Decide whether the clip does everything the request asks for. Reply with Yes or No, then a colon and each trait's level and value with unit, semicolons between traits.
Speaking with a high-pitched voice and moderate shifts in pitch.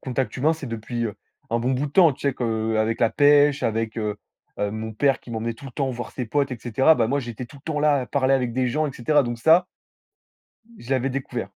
No: low, 125 Hz; average, 3.7 semitones